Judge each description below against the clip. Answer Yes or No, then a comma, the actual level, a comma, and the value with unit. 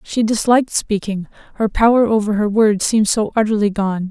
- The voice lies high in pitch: Yes, high, 215 Hz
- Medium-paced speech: Yes, average, 175 wpm